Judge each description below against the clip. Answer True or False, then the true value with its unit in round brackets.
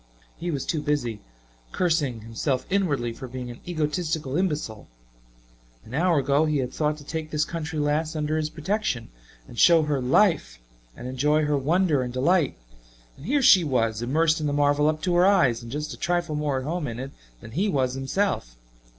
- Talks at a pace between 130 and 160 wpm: False (195 wpm)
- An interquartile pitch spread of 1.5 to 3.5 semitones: False (3.9 semitones)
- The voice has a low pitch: False (150 Hz)